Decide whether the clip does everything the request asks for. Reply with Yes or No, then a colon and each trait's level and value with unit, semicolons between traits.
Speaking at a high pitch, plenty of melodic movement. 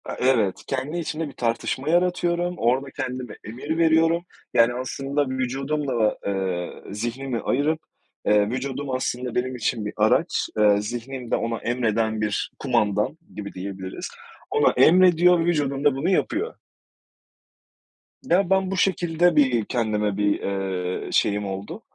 No: low, 130 Hz; wide, 6.5 semitones